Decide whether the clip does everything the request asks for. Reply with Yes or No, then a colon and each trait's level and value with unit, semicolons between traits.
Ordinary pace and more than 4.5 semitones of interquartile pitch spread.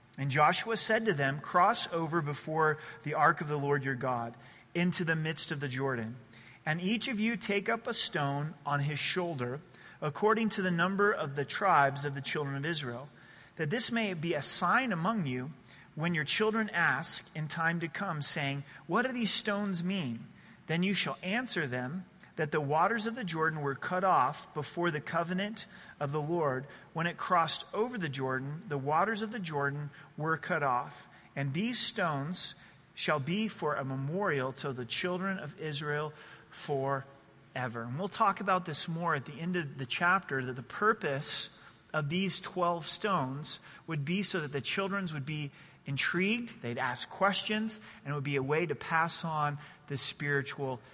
Yes: average, 185 wpm; average, 4.9 semitones